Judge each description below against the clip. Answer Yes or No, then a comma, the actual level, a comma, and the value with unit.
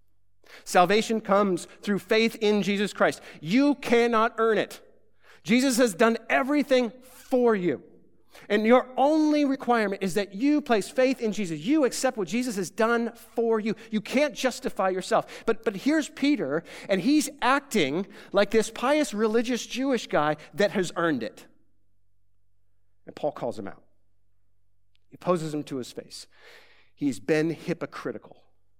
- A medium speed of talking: Yes, average, 150 wpm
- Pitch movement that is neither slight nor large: No, wide, 7.0 semitones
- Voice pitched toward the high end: Yes, high, 220 Hz